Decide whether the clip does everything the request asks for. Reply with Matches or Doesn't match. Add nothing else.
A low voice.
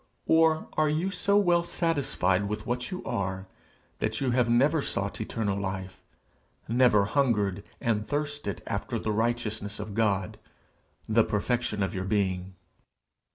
Matches